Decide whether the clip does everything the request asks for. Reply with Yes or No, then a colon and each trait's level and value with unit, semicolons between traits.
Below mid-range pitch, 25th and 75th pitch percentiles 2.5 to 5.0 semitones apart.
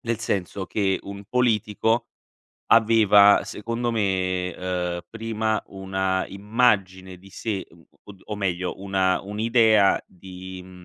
Yes: low, 100 Hz; average, 2.9 semitones